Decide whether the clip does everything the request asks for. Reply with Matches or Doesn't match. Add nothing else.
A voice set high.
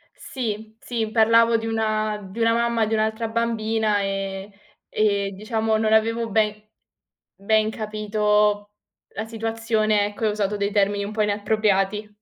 Matches